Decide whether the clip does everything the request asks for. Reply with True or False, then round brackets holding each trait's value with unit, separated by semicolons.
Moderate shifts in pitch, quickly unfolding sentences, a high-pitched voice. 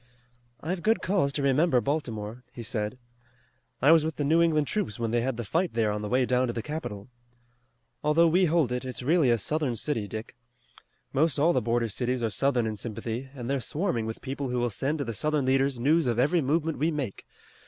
False (4.7 semitones; 220 wpm; 130 Hz)